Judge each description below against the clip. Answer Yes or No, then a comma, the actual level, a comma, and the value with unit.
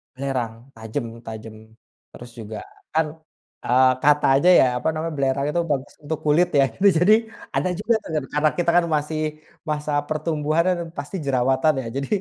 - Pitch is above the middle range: No, medium, 145 Hz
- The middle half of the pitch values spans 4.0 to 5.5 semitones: No, average, 3.2 semitones